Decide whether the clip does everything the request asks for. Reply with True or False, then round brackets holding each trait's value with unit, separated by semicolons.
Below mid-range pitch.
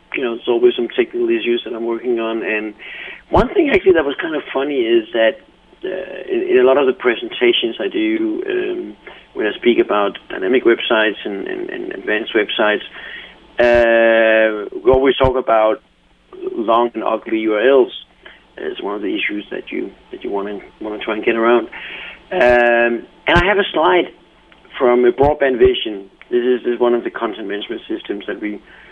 False (175 Hz)